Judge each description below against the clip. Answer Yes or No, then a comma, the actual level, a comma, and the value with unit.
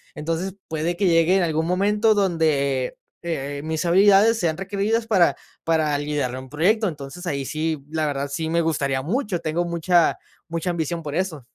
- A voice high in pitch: No, medium, 165 Hz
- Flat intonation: No, average, 3.6 semitones